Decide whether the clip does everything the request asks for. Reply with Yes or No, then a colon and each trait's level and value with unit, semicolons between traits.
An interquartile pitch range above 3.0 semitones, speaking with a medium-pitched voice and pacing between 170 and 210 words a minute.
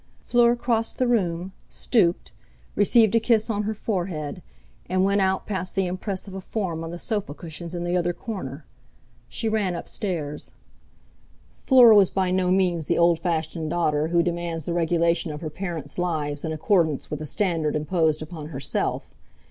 Yes: average, 3.6 semitones; medium, 175 Hz; average, 175 wpm